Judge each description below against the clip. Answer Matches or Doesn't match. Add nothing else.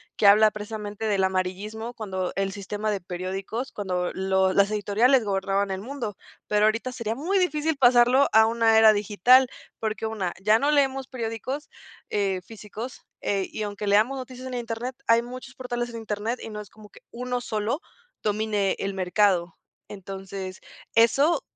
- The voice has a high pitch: Matches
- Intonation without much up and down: Doesn't match